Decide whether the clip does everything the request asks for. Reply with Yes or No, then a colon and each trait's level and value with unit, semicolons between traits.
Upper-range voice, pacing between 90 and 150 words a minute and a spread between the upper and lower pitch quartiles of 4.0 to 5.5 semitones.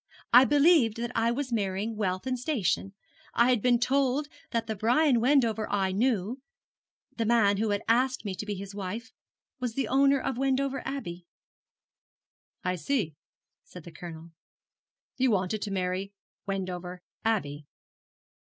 Yes: high, 225 Hz; average, 145 wpm; average, 5.0 semitones